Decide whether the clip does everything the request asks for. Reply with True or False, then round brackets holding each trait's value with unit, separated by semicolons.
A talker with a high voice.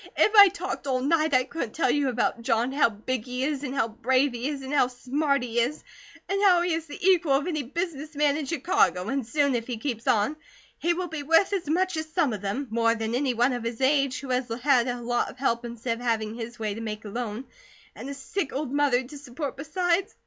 True (270 Hz)